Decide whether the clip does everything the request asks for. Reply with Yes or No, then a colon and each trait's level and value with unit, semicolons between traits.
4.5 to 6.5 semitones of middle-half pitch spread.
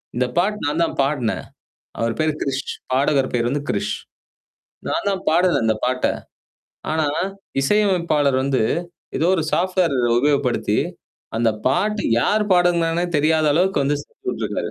Yes: average, 4.9 semitones